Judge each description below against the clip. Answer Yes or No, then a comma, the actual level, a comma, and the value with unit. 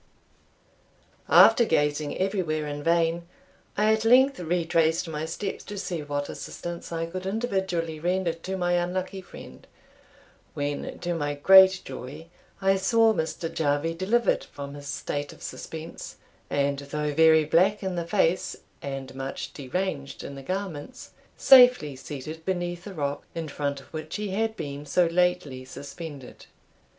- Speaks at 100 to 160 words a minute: Yes, average, 145 wpm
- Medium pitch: Yes, medium, 165 Hz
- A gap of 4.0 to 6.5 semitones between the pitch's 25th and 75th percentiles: Yes, average, 4.4 semitones